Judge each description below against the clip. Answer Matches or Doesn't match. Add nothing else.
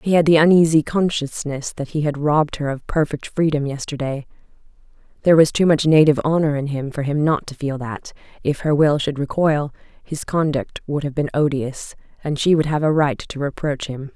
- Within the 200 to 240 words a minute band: Matches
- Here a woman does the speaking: Matches